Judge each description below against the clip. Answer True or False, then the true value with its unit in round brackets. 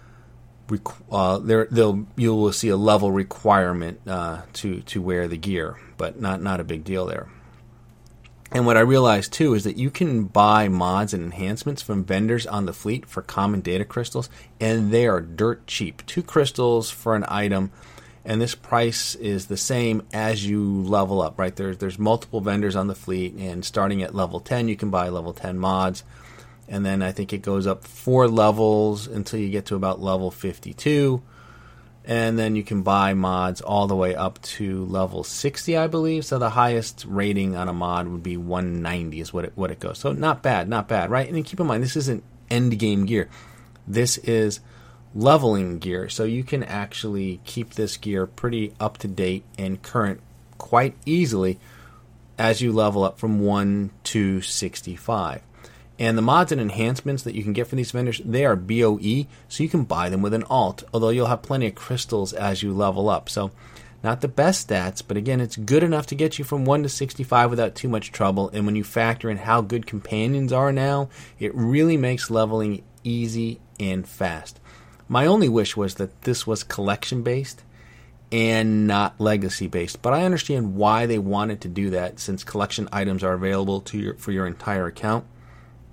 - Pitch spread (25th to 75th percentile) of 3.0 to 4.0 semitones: True (3.5 semitones)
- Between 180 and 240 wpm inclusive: True (190 wpm)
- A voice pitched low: True (110 Hz)